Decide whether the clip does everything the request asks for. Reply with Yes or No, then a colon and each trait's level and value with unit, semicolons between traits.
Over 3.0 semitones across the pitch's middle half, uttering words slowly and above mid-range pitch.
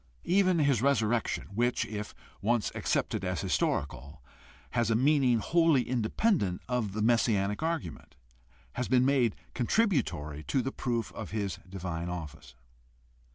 No: wide, 5.4 semitones; slow, 130 wpm; low, 120 Hz